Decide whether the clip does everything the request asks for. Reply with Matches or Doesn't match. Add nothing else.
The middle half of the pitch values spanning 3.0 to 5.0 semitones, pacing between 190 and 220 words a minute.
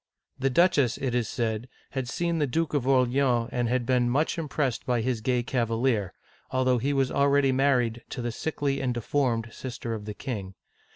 Doesn't match